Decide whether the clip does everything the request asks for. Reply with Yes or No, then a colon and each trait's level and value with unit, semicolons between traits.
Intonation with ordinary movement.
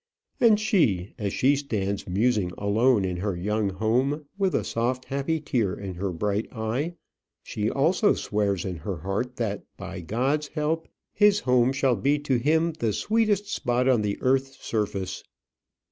No: wide, 6.3 semitones